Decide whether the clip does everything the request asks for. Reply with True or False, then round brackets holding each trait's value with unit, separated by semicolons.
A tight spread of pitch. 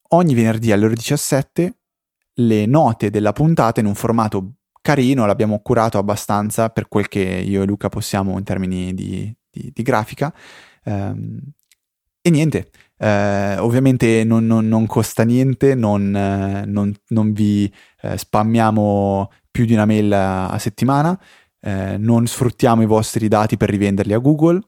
False (3.2 semitones)